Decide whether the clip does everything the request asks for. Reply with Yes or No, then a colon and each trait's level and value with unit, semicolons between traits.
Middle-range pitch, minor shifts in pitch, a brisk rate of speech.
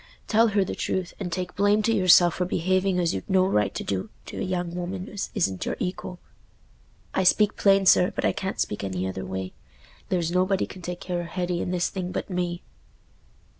Yes: medium, 180 Hz; narrow, 1.7 semitones; fast, 210 wpm